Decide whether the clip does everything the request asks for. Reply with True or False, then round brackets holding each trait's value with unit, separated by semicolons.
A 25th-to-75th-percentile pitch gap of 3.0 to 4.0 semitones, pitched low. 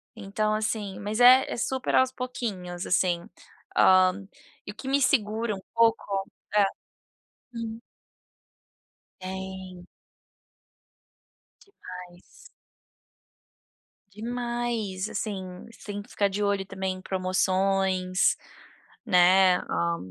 False (3.3 semitones; 195 Hz)